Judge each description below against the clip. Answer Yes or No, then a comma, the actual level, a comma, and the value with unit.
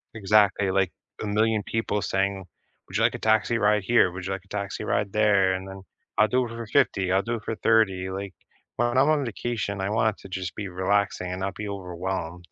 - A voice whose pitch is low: Yes, low, 100 Hz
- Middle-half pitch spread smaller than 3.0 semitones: Yes, narrow, 2.5 semitones